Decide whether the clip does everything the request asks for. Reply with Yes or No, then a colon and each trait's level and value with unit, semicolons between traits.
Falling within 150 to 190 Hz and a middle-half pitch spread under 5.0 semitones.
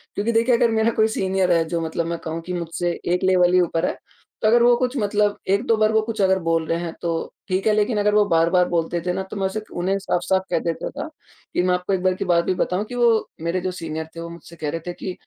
Yes: medium, 185 Hz; average, 3.7 semitones